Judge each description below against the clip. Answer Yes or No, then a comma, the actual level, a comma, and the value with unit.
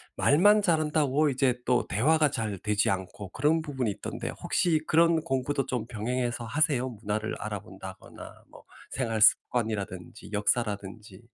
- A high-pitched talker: No, low, 125 Hz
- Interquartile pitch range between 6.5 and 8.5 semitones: No, wide, 5.7 semitones